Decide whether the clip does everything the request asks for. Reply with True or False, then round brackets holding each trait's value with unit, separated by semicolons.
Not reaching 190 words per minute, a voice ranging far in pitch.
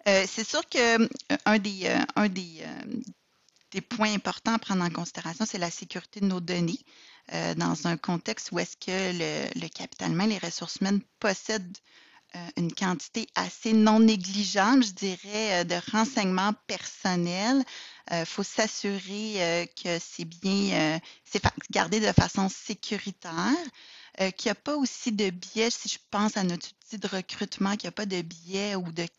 False (180 wpm; 3.7 semitones)